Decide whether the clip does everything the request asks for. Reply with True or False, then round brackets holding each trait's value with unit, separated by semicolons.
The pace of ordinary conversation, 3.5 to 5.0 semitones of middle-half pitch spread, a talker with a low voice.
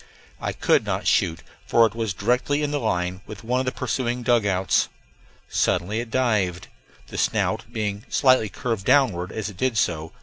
True (170 wpm; 4.6 semitones; 110 Hz)